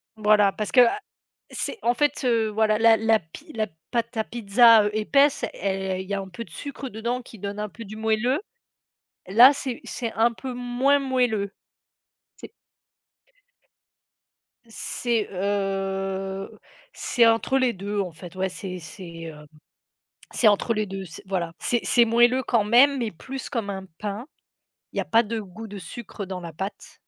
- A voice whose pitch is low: No, high, 215 Hz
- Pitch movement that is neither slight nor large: Yes, average, 3.7 semitones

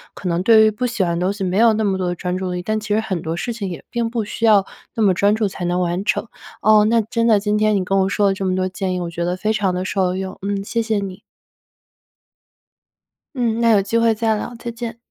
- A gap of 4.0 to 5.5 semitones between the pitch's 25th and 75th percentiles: No, average, 3.0 semitones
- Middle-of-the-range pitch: No, high, 200 Hz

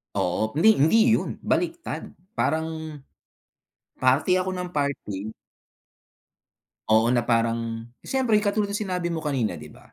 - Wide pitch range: Yes, wide, 8.0 semitones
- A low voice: No, medium, 150 Hz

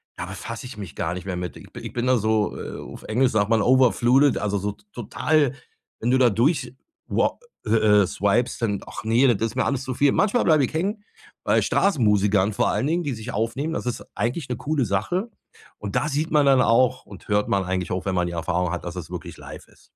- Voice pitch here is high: No, low, 115 Hz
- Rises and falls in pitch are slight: No, average, 4.9 semitones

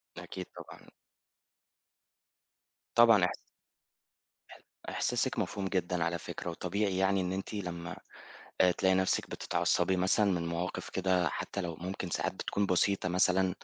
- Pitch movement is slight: Yes, narrow, 1.5 semitones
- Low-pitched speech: Yes, very low, 95 Hz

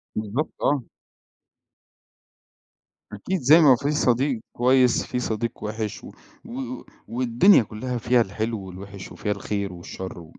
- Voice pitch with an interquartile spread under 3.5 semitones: No, average, 4.2 semitones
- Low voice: Yes, low, 115 Hz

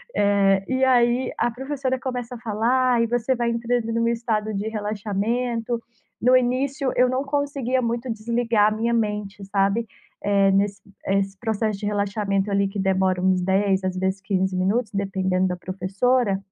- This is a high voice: Yes, high, 215 Hz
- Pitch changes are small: No, average, 3.7 semitones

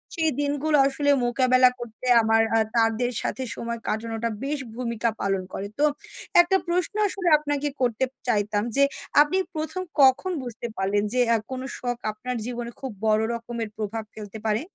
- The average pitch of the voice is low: No, high, 240 Hz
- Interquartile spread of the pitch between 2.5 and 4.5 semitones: Yes, average, 4.2 semitones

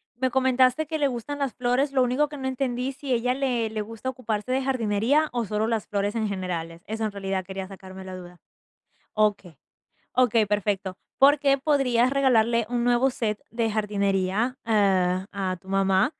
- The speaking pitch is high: Yes, high, 230 Hz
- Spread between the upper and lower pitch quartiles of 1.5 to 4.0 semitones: No, average, 4.6 semitones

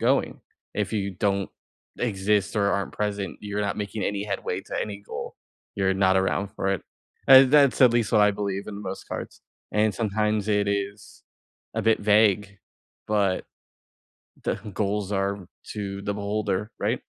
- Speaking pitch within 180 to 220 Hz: No, low, 100 Hz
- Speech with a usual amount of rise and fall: No, narrow, 1.3 semitones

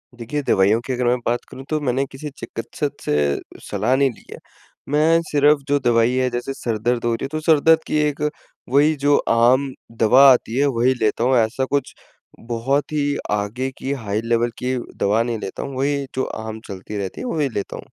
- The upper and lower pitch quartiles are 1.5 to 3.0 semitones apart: No, average, 3.7 semitones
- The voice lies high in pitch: No, low, 130 Hz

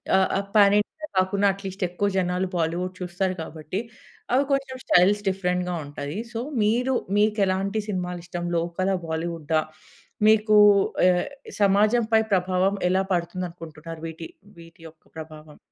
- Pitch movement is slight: No, average, 3.0 semitones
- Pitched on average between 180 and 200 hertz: Yes, medium, 185 Hz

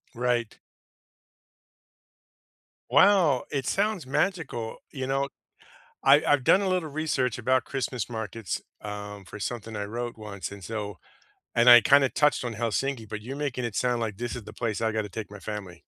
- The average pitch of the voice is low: Yes, low, 120 Hz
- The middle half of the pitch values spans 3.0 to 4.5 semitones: Yes, average, 4.2 semitones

